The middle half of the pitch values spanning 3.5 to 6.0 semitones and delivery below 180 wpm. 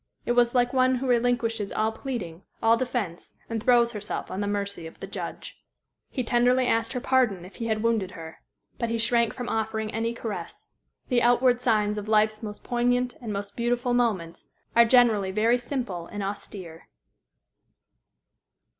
No: average, 2.9 semitones; average, 170 wpm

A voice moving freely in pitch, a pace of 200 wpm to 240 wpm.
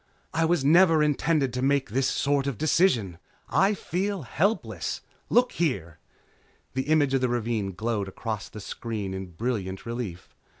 No: wide, 6.7 semitones; average, 160 wpm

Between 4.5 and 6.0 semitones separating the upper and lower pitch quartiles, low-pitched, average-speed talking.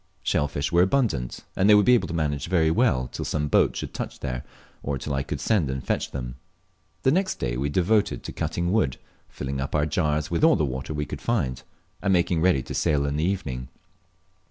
No: wide, 5.6 semitones; very low, 75 Hz; fast, 225 wpm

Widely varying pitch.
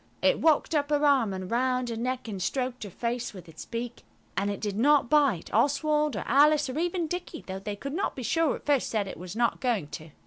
Yes: wide, 6.1 semitones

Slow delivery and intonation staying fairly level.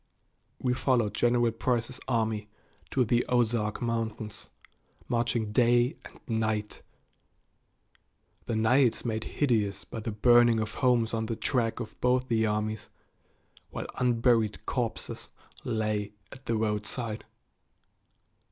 Yes: slow, 115 wpm; narrow, 1.9 semitones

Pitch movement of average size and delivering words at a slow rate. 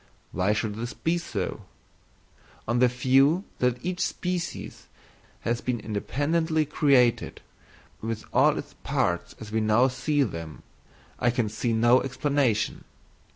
Yes: average, 4.6 semitones; slow, 130 wpm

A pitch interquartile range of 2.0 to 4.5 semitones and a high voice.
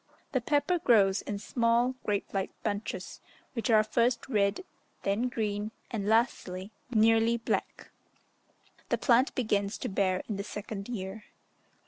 Yes: average, 2.9 semitones; high, 215 Hz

